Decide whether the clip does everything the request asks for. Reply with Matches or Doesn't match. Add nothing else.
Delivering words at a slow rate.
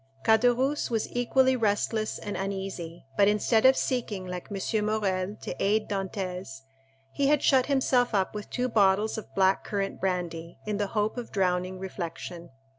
Doesn't match